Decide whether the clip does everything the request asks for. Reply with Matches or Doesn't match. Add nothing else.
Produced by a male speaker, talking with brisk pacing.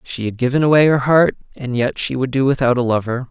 Matches